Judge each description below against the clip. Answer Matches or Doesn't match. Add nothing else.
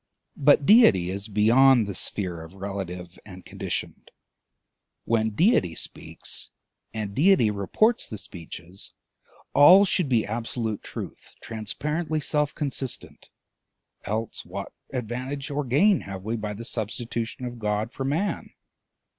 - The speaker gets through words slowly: Matches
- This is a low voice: Matches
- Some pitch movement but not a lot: Doesn't match